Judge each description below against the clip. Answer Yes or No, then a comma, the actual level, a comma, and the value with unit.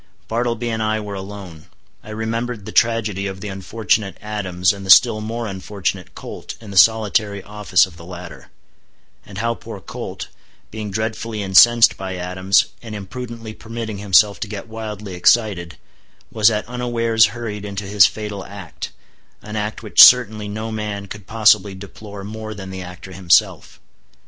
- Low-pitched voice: Yes, low, 105 Hz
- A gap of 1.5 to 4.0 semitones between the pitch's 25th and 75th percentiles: Yes, narrow, 2.5 semitones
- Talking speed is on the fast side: No, average, 160 wpm